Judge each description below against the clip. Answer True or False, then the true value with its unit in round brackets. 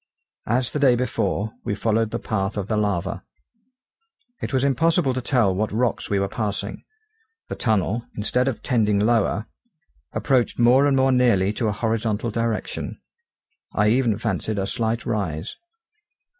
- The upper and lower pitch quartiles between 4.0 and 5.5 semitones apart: False (3.3 semitones)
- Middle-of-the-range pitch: False (110 Hz)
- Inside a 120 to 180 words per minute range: True (155 wpm)